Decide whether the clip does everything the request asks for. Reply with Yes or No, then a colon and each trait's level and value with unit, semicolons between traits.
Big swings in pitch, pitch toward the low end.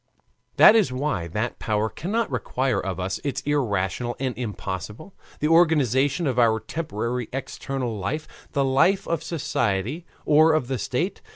Yes: wide, 5.9 semitones; low, 130 Hz